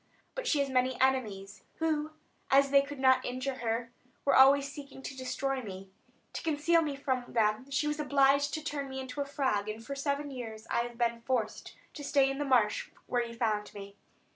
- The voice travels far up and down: No, average, 3.1 semitones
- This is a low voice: No, very high, 265 Hz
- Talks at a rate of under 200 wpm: No, fast, 205 wpm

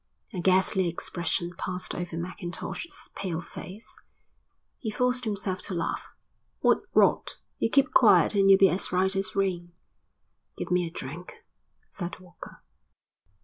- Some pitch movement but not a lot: No, narrow, 2.2 semitones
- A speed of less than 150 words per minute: Yes, average, 140 wpm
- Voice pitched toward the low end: No, medium, 185 Hz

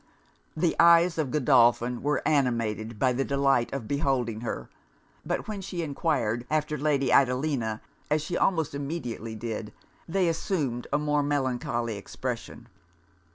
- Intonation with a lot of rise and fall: No, average, 4.4 semitones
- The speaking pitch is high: No, medium, 140 Hz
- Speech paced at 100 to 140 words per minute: Yes, slow, 135 wpm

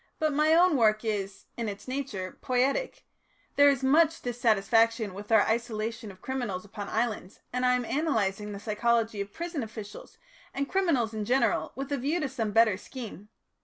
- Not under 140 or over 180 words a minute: Yes, average, 175 wpm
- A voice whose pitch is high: Yes, high, 230 Hz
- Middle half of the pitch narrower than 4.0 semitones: No, average, 4.4 semitones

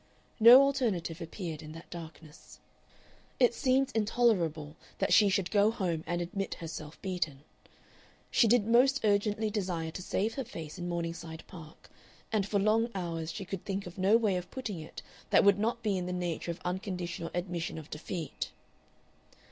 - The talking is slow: No, average, 170 wpm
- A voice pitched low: No, medium, 185 Hz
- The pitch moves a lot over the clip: No, average, 4.4 semitones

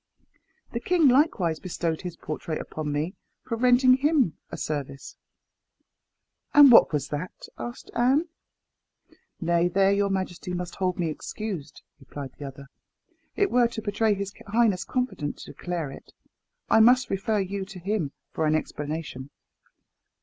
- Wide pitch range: Yes, wide, 6.8 semitones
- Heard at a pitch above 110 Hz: Yes, medium, 185 Hz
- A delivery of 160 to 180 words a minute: No, average, 140 wpm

